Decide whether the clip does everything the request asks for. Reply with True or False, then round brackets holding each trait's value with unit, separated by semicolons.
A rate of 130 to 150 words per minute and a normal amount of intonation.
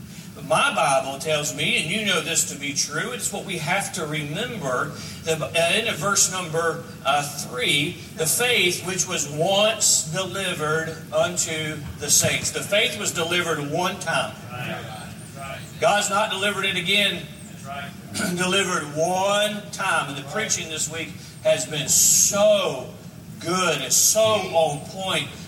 True (135 wpm; 3.7 semitones)